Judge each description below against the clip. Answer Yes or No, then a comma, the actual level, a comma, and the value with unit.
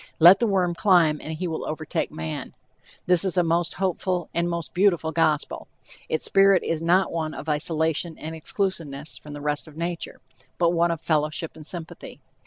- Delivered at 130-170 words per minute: No, average, 185 wpm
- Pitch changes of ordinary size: No, narrow, 2.2 semitones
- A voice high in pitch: No, medium, 165 Hz